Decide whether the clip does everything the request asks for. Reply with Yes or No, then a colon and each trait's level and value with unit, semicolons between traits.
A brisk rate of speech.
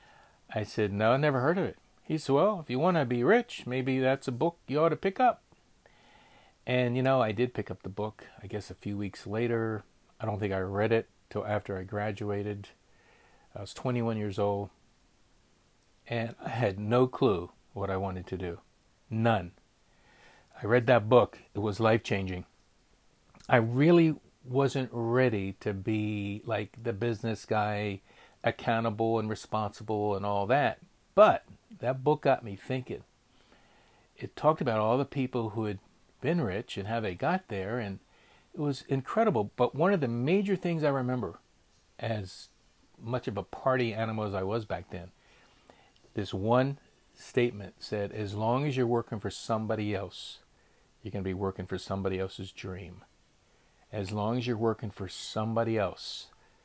No: average, 175 wpm